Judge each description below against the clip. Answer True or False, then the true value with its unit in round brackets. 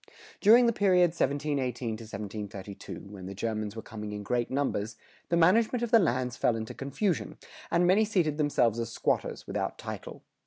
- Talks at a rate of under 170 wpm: False (180 wpm)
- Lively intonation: True (8.6 semitones)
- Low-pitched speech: True (130 Hz)